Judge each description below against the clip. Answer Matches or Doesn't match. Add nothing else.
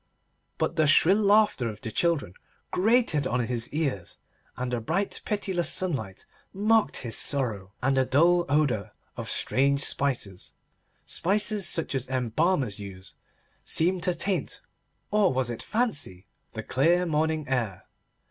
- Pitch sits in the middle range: Matches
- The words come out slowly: Matches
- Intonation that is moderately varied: Doesn't match